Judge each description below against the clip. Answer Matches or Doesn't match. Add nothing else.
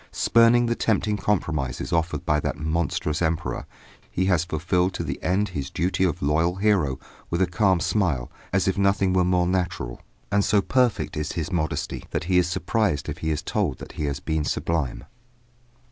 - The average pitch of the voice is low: Matches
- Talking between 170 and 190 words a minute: Matches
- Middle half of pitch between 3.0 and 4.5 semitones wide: Matches